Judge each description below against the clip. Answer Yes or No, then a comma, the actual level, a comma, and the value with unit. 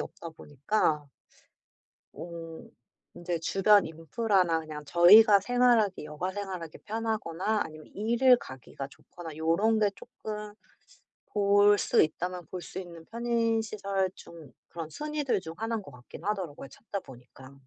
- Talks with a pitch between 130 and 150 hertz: No, high, 190 Hz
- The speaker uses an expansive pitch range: No, average, 4.9 semitones